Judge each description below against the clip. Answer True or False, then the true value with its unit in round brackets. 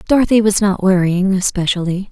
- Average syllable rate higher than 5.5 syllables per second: True (5.7 syllables/s)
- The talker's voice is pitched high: True (195 Hz)